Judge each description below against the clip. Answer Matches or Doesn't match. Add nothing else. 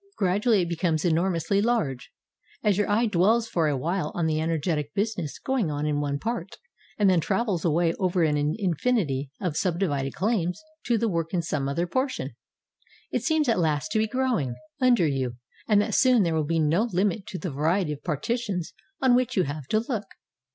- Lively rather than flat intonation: Matches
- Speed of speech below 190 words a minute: Doesn't match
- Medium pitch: Matches